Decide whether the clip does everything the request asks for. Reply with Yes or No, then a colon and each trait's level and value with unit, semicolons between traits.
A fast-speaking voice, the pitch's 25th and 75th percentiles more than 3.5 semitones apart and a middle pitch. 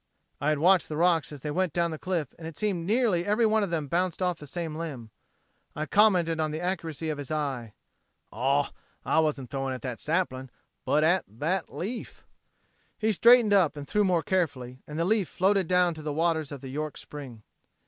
Yes: fast, 210 wpm; average, 4.1 semitones; medium, 160 Hz